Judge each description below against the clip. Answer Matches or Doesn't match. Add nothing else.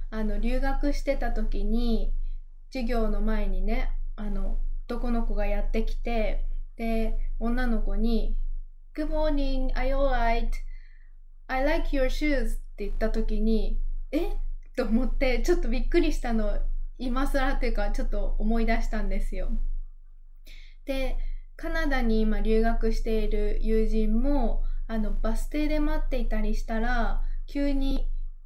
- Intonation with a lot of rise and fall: Doesn't match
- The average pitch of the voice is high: Matches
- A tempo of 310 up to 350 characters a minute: Doesn't match